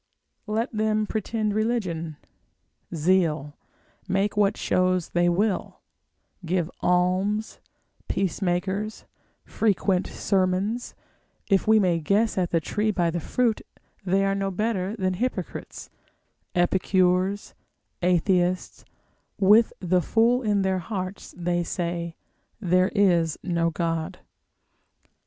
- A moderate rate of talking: No, slow, 110 wpm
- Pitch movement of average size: Yes, average, 3.0 semitones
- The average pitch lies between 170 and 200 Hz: Yes, medium, 185 Hz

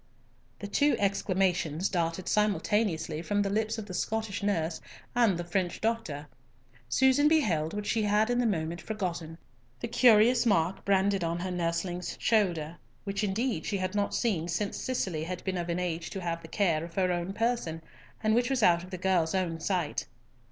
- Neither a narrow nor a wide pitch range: Yes, average, 4.0 semitones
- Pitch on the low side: No, high, 190 Hz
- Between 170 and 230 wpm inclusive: Yes, average, 185 wpm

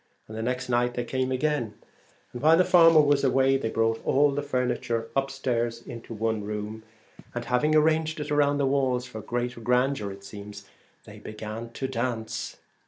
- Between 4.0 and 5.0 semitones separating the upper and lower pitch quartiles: No, average, 3.6 semitones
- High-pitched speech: No, low, 125 Hz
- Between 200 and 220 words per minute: No, average, 175 wpm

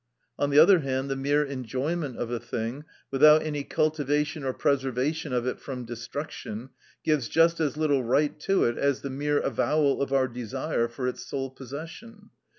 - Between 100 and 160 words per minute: No, average, 180 wpm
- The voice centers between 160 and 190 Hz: No, medium, 140 Hz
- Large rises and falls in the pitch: No, average, 2.9 semitones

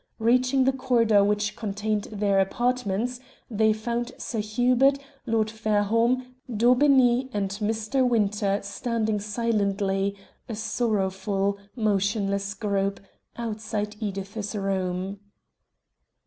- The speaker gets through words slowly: Yes, slow, 95 wpm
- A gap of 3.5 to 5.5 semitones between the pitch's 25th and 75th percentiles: No, average, 2.9 semitones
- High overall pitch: Yes, high, 215 Hz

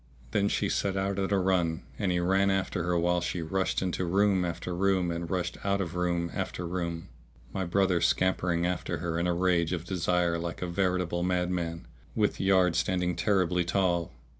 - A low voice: Yes, very low, 90 Hz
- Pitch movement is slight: Yes, narrow, 1.6 semitones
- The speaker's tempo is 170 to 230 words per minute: Yes, average, 190 wpm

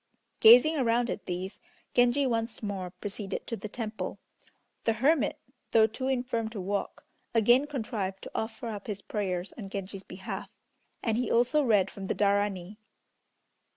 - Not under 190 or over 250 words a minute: No, average, 155 wpm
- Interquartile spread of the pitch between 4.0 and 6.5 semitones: No, average, 3.3 semitones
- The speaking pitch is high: Yes, high, 220 Hz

